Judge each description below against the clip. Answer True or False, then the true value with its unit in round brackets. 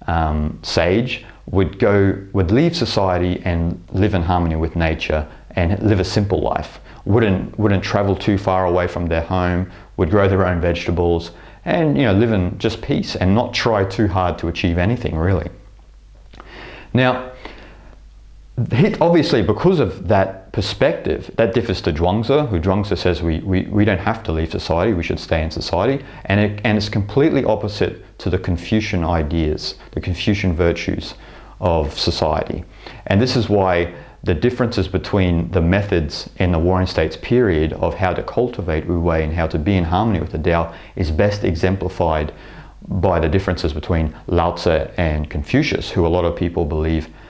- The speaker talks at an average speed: True (170 wpm)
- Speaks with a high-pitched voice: False (90 Hz)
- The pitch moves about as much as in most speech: True (3.6 semitones)